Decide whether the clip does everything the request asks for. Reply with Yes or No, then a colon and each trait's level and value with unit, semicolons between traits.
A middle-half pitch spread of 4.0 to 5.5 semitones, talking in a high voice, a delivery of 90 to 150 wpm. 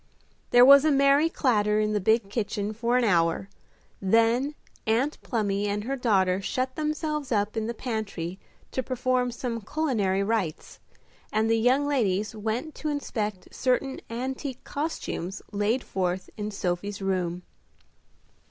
Yes: average, 4.3 semitones; high, 225 Hz; average, 145 wpm